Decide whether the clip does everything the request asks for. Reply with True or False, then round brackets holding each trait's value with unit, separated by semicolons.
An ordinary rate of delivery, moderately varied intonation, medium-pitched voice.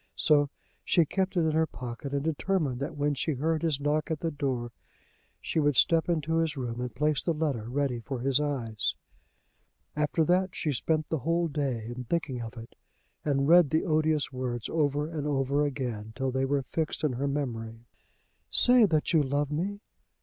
True (190 wpm; 3.6 semitones; 145 Hz)